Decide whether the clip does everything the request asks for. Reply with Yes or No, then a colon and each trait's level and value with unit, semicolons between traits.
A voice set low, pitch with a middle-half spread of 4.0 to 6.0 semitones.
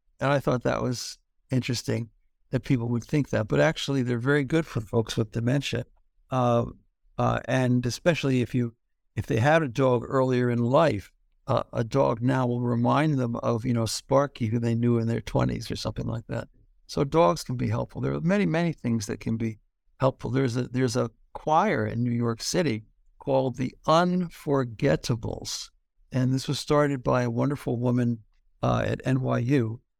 No: low, 125 Hz; average, 2.9 semitones